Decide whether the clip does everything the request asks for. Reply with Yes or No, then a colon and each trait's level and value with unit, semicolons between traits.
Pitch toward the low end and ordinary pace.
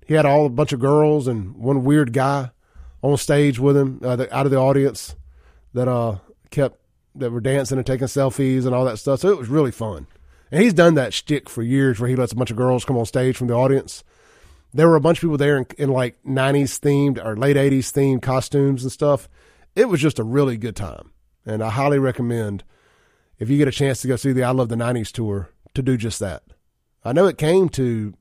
No: low, 130 Hz; fast, 240 wpm